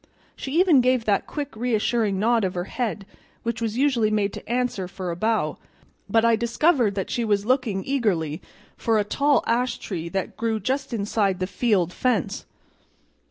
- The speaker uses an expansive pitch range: No, average, 3.9 semitones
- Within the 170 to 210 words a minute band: Yes, average, 175 wpm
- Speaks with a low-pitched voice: No, high, 225 Hz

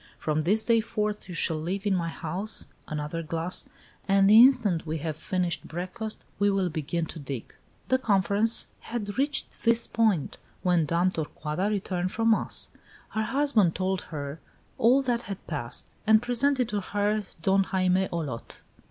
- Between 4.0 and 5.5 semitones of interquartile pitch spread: Yes, average, 4.7 semitones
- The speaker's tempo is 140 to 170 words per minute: Yes, average, 160 wpm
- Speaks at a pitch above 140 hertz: Yes, high, 190 Hz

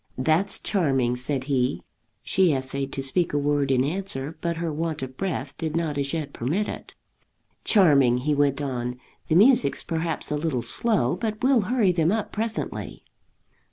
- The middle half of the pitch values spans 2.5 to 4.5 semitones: No, average, 5.3 semitones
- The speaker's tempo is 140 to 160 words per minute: No, average, 170 wpm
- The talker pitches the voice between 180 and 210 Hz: No, medium, 150 Hz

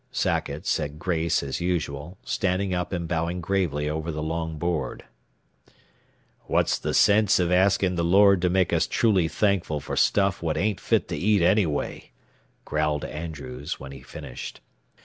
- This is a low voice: Yes, very low, 85 Hz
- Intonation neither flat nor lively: Yes, average, 3.7 semitones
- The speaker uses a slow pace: No, average, 155 wpm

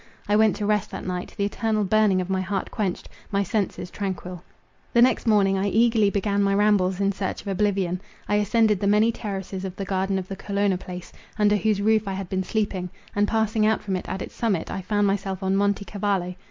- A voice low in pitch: No, high, 200 Hz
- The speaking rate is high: Yes, fast, 220 wpm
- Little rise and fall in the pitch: Yes, narrow, 1.8 semitones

